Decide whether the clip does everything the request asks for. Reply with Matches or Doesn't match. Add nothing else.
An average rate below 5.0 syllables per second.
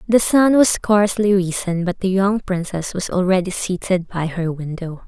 Matches